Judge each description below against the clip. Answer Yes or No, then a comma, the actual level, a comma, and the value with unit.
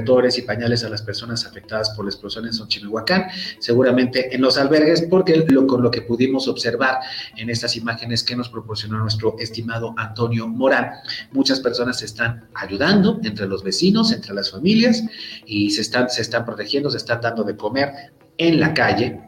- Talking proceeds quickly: No, average, 175 wpm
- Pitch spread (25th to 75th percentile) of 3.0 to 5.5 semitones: Yes, average, 3.8 semitones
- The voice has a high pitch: No, low, 120 Hz